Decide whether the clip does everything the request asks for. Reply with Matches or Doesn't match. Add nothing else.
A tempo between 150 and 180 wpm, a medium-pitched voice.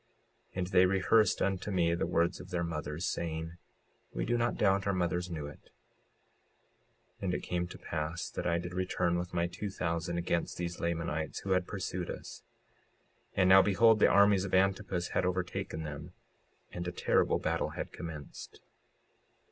Doesn't match